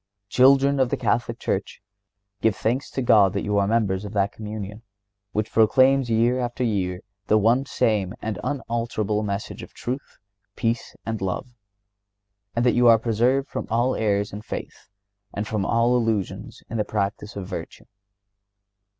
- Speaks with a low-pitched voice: Yes, low, 110 Hz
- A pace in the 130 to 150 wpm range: No, average, 160 wpm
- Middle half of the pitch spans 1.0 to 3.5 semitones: Yes, average, 2.9 semitones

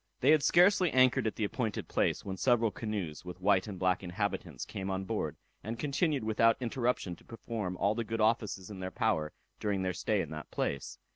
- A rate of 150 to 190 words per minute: No, fast, 205 wpm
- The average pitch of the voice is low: Yes, low, 105 Hz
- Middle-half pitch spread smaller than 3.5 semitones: No, average, 4.0 semitones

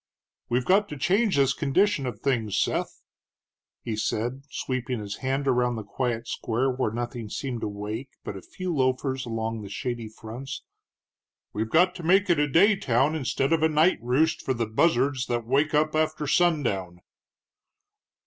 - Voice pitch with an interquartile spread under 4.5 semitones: No, average, 5.0 semitones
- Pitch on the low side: Yes, low, 130 Hz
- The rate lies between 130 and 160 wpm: No, average, 170 wpm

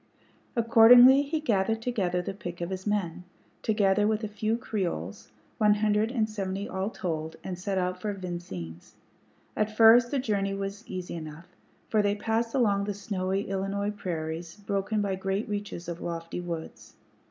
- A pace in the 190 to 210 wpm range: No, average, 165 wpm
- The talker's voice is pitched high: Yes, high, 200 Hz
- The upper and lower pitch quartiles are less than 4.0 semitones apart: Yes, average, 3.2 semitones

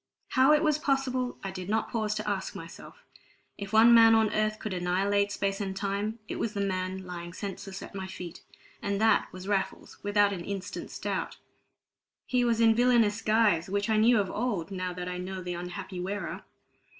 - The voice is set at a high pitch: Yes, high, 200 Hz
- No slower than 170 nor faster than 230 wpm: Yes, average, 195 wpm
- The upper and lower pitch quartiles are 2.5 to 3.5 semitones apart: Yes, average, 3.0 semitones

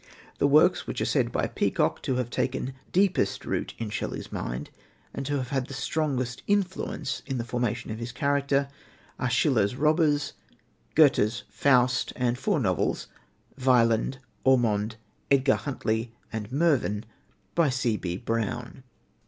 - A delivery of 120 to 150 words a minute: Yes, average, 140 wpm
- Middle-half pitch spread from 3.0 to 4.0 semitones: Yes, average, 3.6 semitones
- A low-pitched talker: Yes, low, 130 Hz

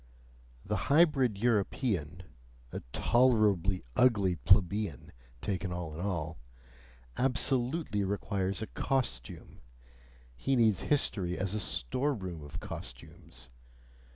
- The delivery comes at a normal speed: No, slow, 95 wpm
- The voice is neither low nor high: No, low, 100 Hz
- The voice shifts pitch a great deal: Yes, wide, 5.7 semitones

